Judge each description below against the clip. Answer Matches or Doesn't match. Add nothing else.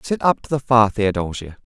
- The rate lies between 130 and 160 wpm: Doesn't match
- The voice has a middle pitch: Doesn't match